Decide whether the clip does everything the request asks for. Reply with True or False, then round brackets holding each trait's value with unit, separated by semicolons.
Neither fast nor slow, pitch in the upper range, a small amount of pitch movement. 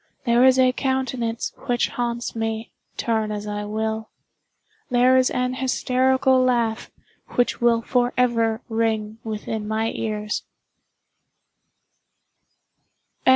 False (105 wpm; 235 Hz; 2.3 semitones)